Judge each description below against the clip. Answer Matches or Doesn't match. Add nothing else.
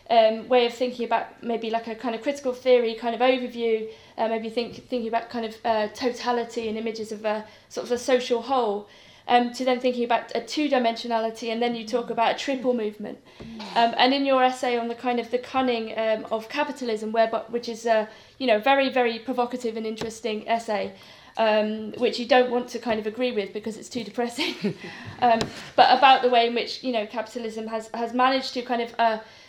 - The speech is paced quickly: Matches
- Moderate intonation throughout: Doesn't match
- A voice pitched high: Matches